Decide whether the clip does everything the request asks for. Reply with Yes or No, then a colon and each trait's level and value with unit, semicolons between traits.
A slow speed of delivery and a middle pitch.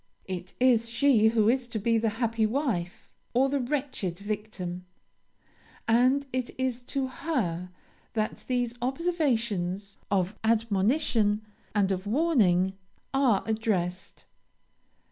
No: slow, 115 wpm; high, 225 Hz